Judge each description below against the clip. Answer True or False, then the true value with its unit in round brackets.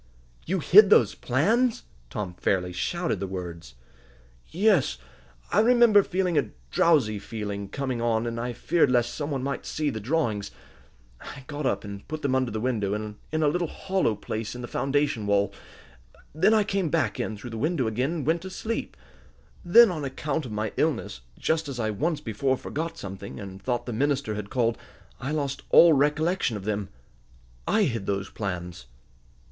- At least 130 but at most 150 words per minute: False (180 wpm)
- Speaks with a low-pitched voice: True (130 Hz)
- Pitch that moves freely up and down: True (7.2 semitones)